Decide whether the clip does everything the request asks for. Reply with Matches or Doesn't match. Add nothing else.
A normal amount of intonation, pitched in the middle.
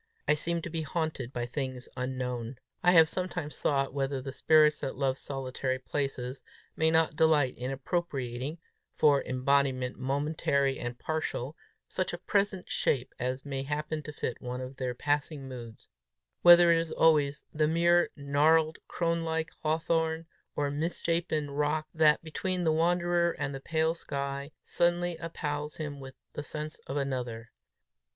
Matches